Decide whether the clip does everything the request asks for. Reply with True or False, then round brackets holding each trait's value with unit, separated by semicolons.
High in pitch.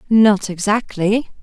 True (210 Hz)